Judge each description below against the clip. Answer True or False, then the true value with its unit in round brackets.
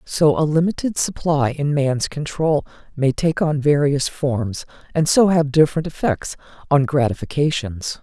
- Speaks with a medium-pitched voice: True (150 Hz)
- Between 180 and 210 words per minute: False (140 wpm)